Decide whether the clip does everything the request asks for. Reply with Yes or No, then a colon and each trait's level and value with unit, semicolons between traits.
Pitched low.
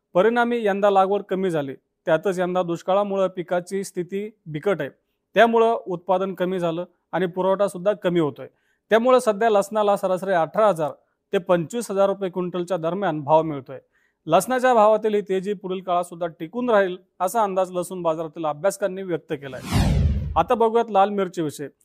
No: medium, 185 Hz